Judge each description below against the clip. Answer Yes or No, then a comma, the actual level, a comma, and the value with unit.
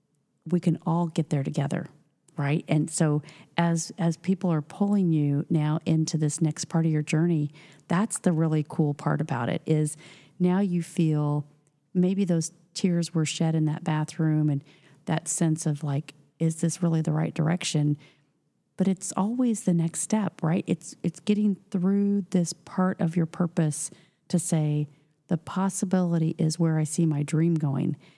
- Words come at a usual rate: Yes, average, 170 wpm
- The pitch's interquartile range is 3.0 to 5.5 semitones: No, narrow, 2.6 semitones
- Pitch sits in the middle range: Yes, medium, 165 Hz